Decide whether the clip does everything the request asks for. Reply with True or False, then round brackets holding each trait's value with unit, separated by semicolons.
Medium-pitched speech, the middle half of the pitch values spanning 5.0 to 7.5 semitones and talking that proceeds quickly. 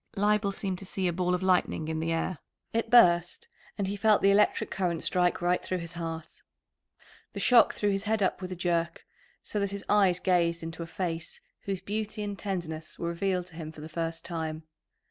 False (180 Hz; 3.0 semitones; 210 wpm)